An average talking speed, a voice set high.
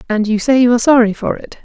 No: fast, 295 wpm; high, 235 Hz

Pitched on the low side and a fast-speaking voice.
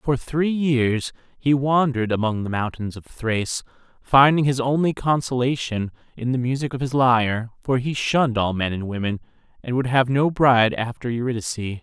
No: low, 125 Hz; average, 170 wpm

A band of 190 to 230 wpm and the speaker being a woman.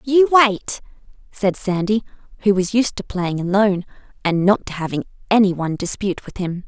No: average, 170 wpm; female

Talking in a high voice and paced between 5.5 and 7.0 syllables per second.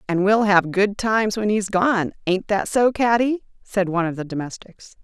No: high, 200 Hz; 4.9 syllables/s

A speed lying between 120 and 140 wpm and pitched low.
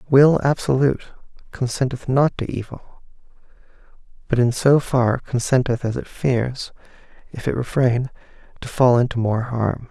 Yes: slow, 135 wpm; low, 125 Hz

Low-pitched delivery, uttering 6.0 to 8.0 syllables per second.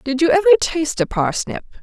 No: very high, 300 Hz; 6.4 syllables/s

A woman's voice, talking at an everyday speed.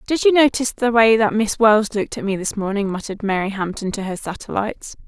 No: female; fast, 225 wpm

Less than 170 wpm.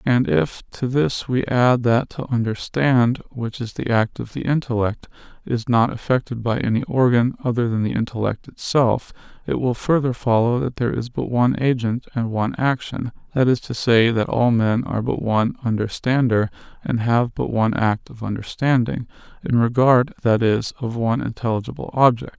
No: average, 175 wpm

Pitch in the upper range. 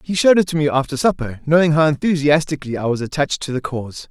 No: medium, 150 Hz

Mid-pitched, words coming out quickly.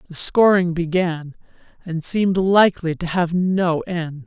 No: medium, 175 Hz; average, 140 wpm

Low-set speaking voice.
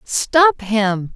No: high, 245 Hz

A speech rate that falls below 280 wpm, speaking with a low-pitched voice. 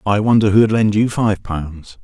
Yes: fast, 205 wpm; low, 105 Hz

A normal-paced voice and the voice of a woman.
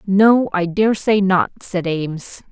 Yes: average, 165 wpm; female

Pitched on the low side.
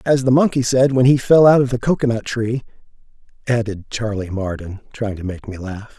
Yes: low, 115 Hz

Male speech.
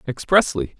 Yes: male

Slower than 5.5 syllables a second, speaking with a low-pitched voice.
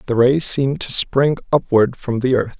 Yes: 4.9 syllables/s; low, 130 Hz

